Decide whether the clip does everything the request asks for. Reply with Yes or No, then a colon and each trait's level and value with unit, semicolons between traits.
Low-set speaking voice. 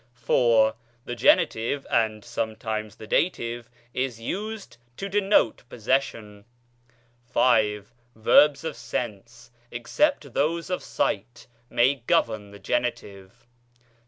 Yes: low, 120 Hz